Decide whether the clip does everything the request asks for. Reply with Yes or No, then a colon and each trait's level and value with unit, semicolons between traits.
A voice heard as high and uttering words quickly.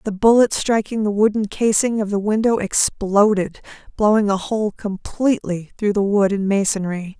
No: high, 205 Hz; average, 160 wpm